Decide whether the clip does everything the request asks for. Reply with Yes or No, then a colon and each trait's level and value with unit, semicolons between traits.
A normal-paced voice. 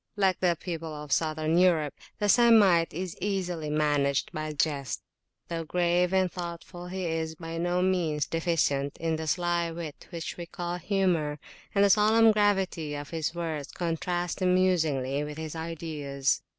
Yes: average, 160 wpm